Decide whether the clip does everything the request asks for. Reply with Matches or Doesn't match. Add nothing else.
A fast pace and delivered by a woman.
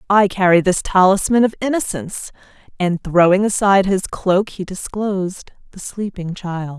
Doesn't match